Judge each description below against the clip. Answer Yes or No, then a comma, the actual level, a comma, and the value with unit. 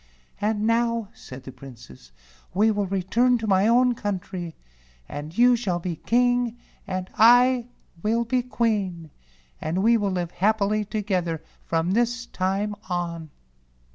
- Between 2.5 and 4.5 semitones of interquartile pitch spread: No, average, 4.9 semitones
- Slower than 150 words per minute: Yes, average, 140 wpm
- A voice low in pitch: No, high, 205 Hz